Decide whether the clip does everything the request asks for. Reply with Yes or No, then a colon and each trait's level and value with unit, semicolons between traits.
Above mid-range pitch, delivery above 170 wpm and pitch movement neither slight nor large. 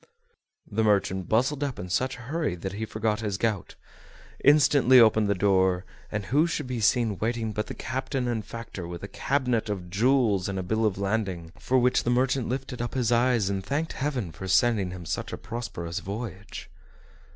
No: low, 110 Hz; average, 195 wpm; average, 4.4 semitones